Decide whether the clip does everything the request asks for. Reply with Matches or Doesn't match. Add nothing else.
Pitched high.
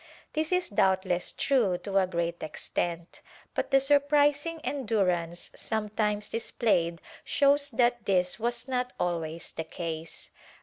Matches